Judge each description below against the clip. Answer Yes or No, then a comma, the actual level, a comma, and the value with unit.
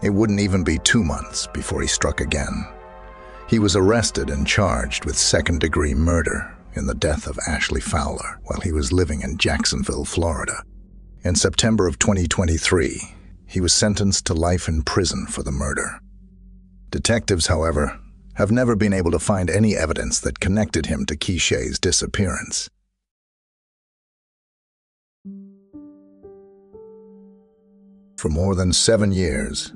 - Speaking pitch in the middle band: No, very low, 95 Hz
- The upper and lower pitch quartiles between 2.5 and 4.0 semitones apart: No, average, 4.4 semitones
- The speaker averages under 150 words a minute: Yes, slow, 135 wpm